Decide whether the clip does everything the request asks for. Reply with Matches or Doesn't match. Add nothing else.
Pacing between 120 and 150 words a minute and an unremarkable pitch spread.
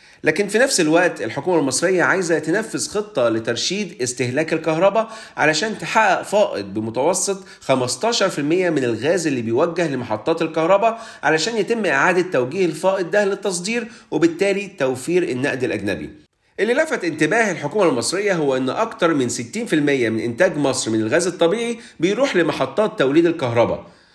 Doesn't match